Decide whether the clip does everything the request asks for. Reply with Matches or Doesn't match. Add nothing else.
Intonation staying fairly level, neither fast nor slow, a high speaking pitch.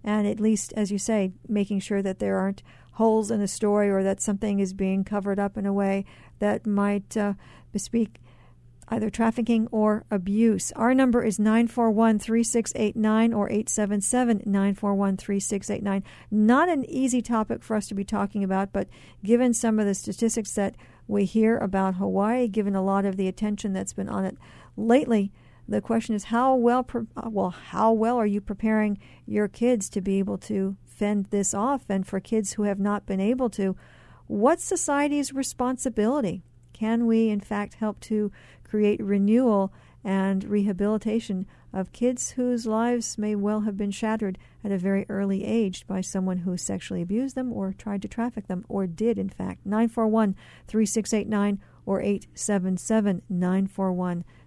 Matches